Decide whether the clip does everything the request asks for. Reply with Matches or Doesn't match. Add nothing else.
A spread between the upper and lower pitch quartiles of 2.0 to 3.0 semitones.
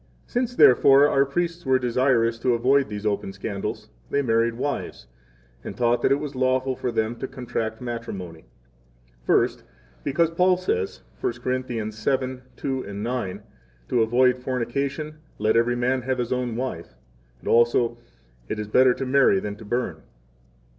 Matches